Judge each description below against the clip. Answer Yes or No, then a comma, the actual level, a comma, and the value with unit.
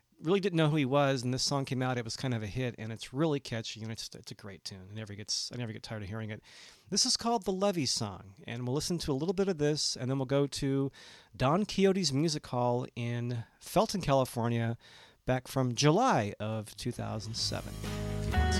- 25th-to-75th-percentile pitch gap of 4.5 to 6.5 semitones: Yes, average, 5.0 semitones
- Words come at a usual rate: No, fast, 235 wpm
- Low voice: Yes, low, 125 Hz